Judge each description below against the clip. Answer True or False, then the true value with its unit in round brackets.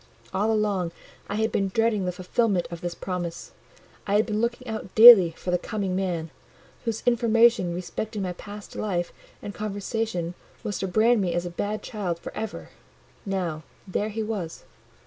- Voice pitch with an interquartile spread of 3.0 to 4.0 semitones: True (3.5 semitones)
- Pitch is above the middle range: True (200 Hz)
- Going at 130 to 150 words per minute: False (165 wpm)